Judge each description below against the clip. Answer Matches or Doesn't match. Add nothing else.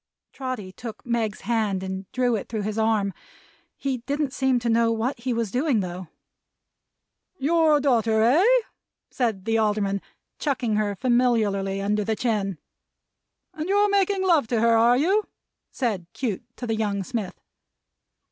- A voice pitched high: Matches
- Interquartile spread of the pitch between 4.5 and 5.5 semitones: Doesn't match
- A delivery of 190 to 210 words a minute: Doesn't match